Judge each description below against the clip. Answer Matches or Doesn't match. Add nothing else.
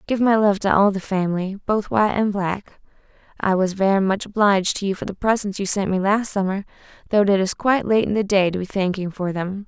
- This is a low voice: Doesn't match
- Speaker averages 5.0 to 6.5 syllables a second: Matches